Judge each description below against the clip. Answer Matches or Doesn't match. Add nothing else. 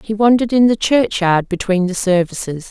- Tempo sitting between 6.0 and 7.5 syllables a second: Doesn't match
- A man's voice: Doesn't match